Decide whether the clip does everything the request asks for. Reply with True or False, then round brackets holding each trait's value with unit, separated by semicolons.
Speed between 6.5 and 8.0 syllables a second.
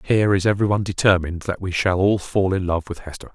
True (6.9 syllables/s)